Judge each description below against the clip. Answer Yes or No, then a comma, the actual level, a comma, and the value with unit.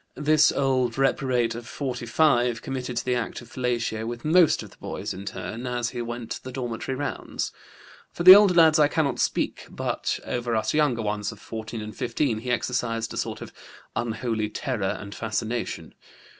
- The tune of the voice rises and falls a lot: No, average, 2.9 semitones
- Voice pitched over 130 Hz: No, low, 120 Hz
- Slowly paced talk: No, average, 175 wpm